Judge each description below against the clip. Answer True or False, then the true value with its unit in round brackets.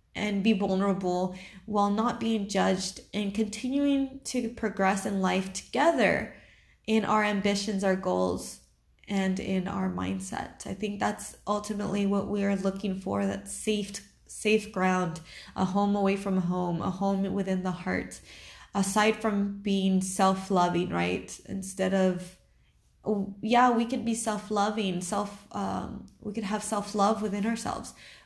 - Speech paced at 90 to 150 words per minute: True (140 wpm)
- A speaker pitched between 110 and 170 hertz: False (200 Hz)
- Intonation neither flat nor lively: False (2.2 semitones)